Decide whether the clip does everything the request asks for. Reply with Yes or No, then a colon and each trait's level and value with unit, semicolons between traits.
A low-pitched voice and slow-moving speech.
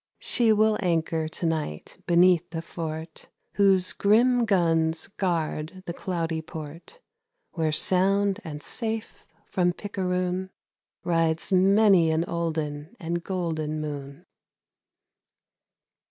No: medium, 170 Hz; slow, 105 wpm